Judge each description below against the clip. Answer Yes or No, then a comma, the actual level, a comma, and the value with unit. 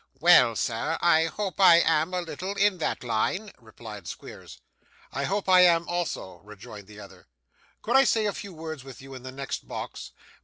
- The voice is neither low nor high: Yes, medium, 160 Hz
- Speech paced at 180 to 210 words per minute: Yes, average, 190 wpm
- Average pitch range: No, wide, 7.7 semitones